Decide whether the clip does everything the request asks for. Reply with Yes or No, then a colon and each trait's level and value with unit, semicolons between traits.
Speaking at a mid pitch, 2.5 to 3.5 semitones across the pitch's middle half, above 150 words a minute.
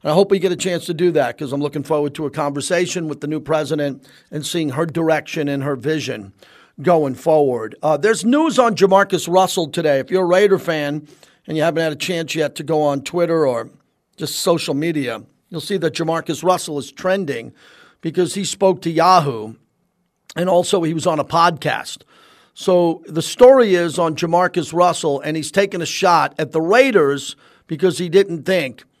Yes: medium, 165 Hz; average, 3.1 semitones; average, 195 wpm